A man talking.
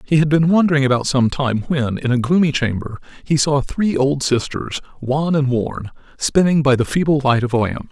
Yes: male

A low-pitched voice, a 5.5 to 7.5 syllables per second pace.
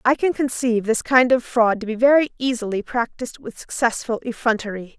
No: high, 240 Hz; 5.6 syllables/s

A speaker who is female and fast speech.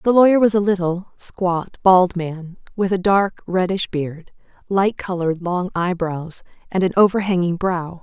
No: female; average, 155 wpm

